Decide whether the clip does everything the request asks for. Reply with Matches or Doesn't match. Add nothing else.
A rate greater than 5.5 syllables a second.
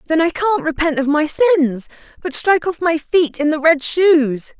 Doesn't match